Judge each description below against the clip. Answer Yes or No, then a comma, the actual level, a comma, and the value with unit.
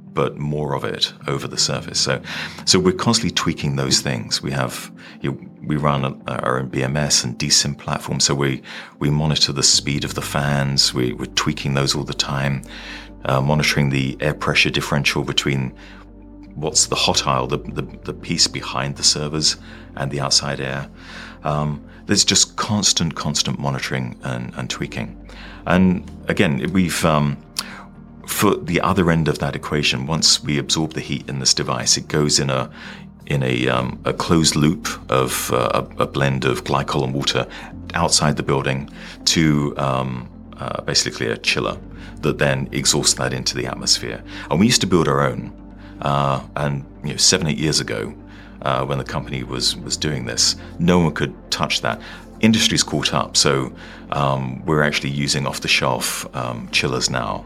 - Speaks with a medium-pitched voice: No, very low, 70 Hz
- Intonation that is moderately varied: No, narrow, 2.2 semitones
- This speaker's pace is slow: No, average, 175 wpm